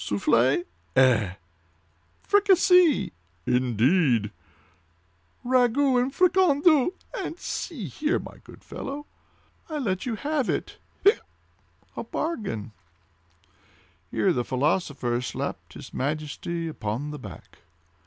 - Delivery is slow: Yes, slow, 90 wpm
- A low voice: No, medium, 185 Hz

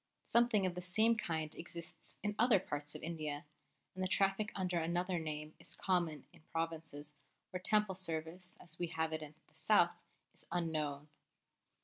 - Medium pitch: Yes, medium, 170 Hz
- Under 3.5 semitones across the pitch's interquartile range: Yes, average, 2.9 semitones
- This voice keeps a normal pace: Yes, average, 165 wpm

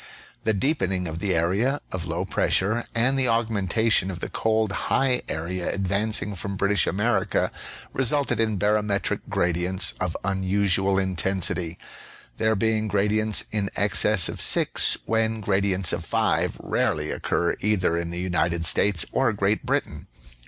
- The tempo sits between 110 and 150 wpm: Yes, average, 145 wpm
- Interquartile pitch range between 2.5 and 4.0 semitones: Yes, average, 3.1 semitones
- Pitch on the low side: Yes, low, 100 Hz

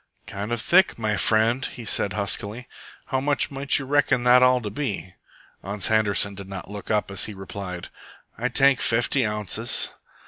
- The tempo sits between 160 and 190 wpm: Yes, average, 175 wpm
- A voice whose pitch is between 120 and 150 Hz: No, low, 110 Hz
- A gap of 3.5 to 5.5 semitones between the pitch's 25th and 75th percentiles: Yes, average, 3.9 semitones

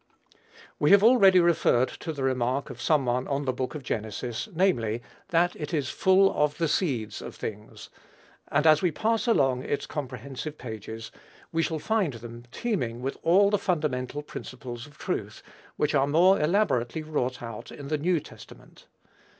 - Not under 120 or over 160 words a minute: No, average, 170 wpm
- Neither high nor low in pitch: Yes, medium, 145 Hz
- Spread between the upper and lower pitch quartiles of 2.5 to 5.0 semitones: No, wide, 5.4 semitones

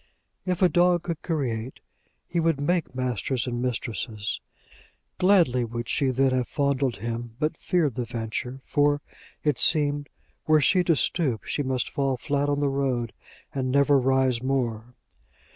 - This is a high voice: No, low, 135 Hz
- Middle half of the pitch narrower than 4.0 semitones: Yes, average, 3.3 semitones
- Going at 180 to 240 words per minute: No, average, 155 wpm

